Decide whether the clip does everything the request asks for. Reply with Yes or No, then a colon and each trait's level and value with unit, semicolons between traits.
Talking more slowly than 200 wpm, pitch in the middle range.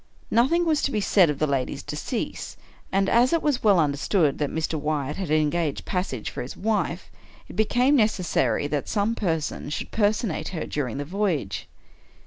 Yes: average, 175 wpm; medium, 175 Hz